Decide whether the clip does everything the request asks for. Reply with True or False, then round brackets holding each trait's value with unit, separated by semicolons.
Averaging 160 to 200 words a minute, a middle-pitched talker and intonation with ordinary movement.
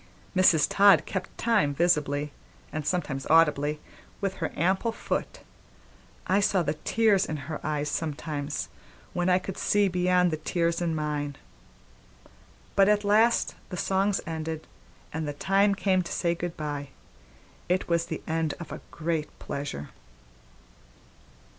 False (140 wpm; 170 Hz; 3.9 semitones)